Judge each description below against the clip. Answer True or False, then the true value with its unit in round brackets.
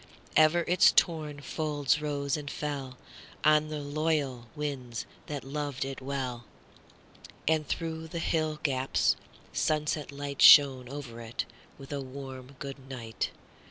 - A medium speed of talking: False (120 wpm)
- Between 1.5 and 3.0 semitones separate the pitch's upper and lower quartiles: True (2.4 semitones)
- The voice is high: False (145 Hz)